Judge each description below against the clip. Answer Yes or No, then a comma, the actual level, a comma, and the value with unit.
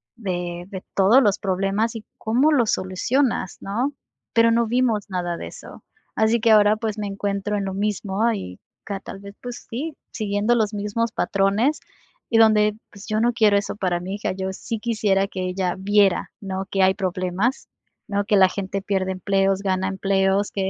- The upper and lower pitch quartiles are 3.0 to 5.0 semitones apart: No, narrow, 2.5 semitones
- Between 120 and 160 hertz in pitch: No, high, 200 Hz